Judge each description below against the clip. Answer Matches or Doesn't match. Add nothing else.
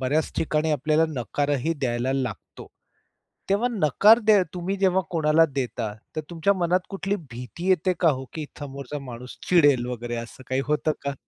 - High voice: Doesn't match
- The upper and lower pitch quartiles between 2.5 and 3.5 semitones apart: Doesn't match